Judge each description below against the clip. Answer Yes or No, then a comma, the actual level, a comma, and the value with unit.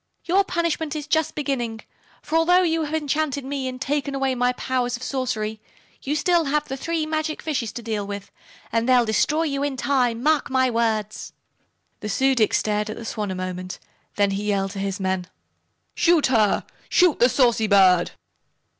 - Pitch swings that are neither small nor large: No, wide, 5.8 semitones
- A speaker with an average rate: Yes, average, 185 wpm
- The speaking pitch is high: Yes, very high, 255 Hz